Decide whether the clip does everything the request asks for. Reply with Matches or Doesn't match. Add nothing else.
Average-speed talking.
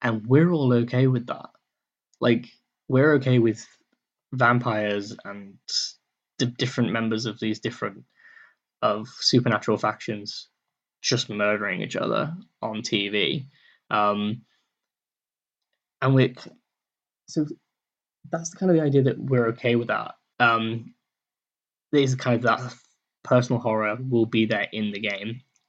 Doesn't match